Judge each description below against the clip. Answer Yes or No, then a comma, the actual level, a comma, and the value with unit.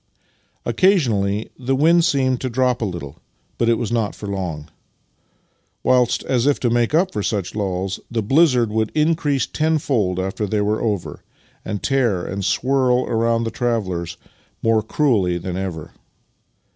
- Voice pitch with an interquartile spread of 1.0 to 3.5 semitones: No, average, 4.9 semitones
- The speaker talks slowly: No, average, 160 wpm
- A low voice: Yes, low, 115 Hz